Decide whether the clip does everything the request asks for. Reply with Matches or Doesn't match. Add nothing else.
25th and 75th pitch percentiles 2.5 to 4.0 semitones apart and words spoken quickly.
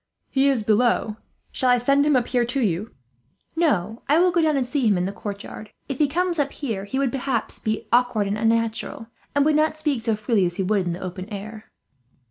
Doesn't match